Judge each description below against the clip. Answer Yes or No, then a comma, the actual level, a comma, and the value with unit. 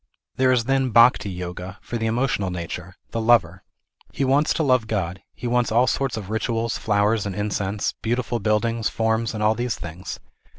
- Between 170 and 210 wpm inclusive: Yes, average, 180 wpm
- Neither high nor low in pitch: No, low, 110 Hz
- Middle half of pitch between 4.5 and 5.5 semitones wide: No, average, 3.2 semitones